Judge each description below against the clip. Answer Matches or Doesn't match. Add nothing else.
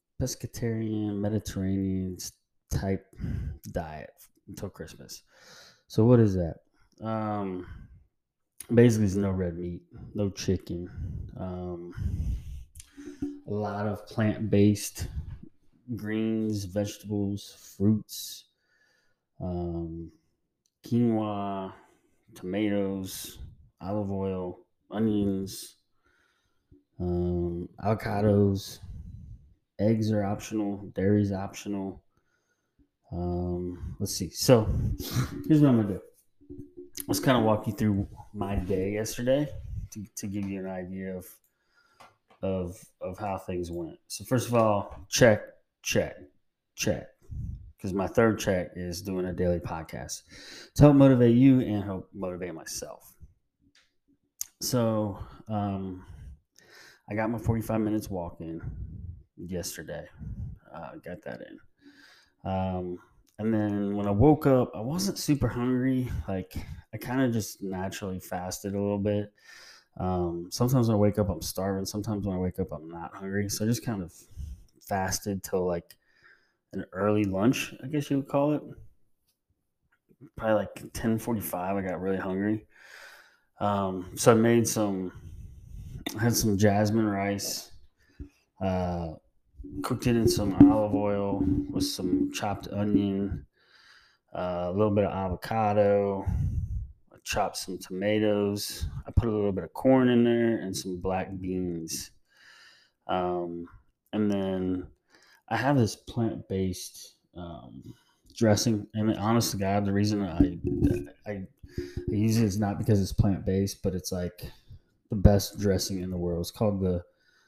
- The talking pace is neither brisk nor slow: Doesn't match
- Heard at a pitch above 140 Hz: Doesn't match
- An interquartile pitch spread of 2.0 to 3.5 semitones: Matches